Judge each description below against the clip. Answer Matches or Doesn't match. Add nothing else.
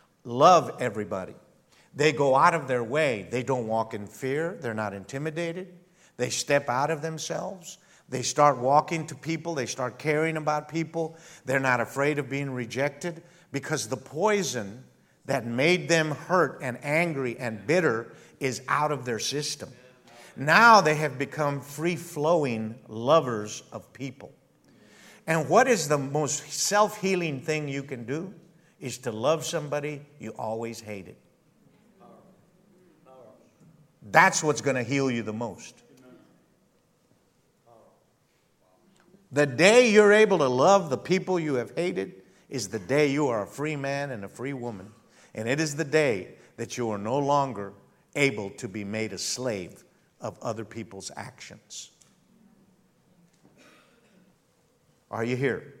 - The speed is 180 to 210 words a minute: Doesn't match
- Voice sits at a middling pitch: Matches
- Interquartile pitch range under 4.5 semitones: Doesn't match